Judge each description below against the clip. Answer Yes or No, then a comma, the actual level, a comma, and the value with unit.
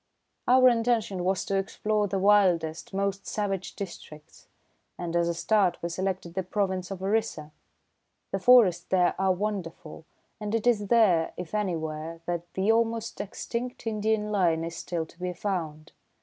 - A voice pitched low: No, high, 190 Hz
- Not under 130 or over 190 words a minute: Yes, average, 155 wpm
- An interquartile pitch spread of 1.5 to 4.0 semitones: Yes, average, 3.7 semitones